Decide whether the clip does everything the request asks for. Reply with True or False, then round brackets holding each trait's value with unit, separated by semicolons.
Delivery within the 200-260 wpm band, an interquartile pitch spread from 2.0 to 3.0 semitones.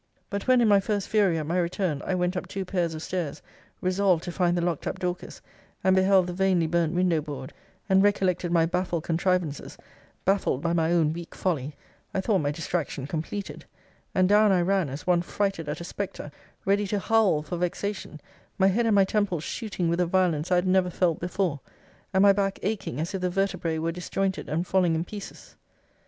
True (205 wpm; 2.6 semitones)